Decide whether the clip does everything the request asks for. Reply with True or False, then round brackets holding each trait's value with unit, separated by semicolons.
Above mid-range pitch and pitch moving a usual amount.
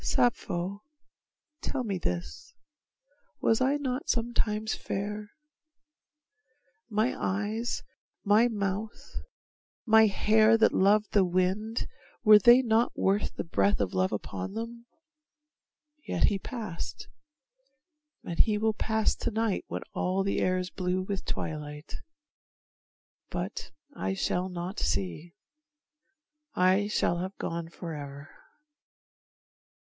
True (200 Hz; 3.8 semitones)